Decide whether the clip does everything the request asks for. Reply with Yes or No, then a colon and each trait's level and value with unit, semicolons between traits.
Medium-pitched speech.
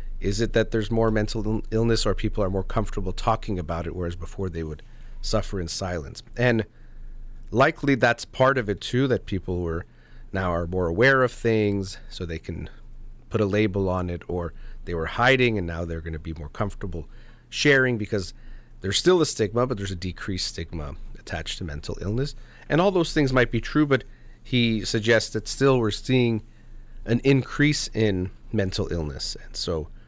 No: low, 110 Hz